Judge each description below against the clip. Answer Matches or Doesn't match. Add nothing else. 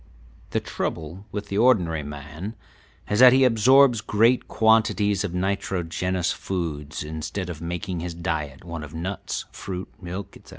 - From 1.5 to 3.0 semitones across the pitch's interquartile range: Doesn't match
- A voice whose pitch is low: Matches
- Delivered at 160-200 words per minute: Doesn't match